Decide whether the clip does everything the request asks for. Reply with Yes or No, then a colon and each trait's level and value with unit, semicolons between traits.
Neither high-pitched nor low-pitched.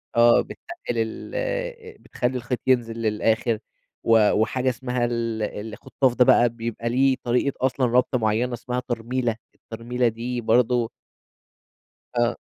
No: low, 120 Hz